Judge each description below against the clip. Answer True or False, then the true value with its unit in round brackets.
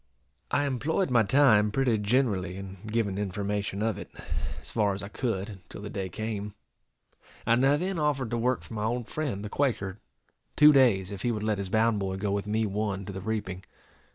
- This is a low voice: True (105 Hz)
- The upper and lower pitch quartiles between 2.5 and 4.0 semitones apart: True (3.7 semitones)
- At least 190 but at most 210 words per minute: True (205 wpm)